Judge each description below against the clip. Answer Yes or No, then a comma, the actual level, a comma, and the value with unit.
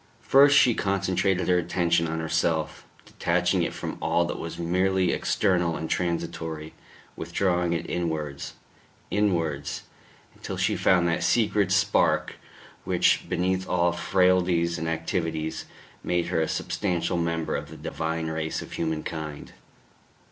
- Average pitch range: No, narrow, 2.2 semitones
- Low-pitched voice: Yes, very low, 85 Hz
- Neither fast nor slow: No, slow, 130 wpm